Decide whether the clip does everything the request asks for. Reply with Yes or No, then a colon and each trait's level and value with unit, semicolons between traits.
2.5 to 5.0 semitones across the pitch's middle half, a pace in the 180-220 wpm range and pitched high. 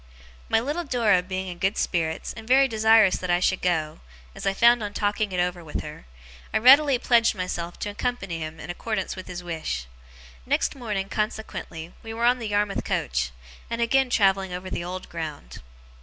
Yes: average, 4.4 semitones; average, 190 wpm; high, 195 Hz